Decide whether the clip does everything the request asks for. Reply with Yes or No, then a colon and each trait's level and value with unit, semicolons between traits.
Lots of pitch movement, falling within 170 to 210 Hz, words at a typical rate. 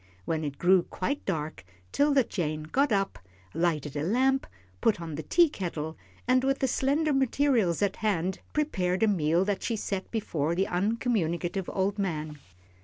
Yes: wide, 7.1 semitones; high, 190 Hz; average, 160 wpm